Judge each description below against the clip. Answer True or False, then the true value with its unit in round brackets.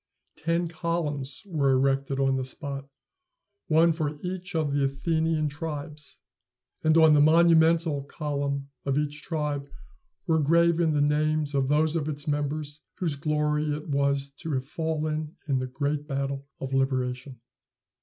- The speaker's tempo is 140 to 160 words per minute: True (145 wpm)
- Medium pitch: True (150 Hz)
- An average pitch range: False (2.3 semitones)